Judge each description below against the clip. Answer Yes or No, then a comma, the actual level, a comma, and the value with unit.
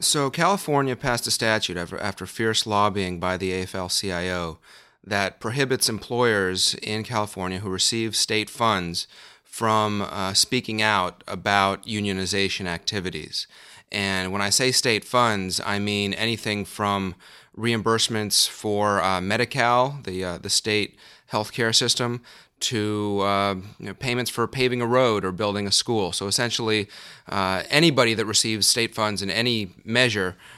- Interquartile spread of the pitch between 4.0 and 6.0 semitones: No, average, 3.2 semitones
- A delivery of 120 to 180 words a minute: Yes, average, 145 wpm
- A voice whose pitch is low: Yes, low, 105 Hz